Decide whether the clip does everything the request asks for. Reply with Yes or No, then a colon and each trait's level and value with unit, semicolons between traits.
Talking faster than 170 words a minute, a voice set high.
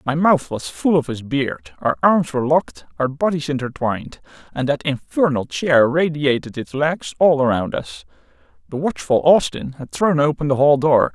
No: average, 180 wpm; low, 135 Hz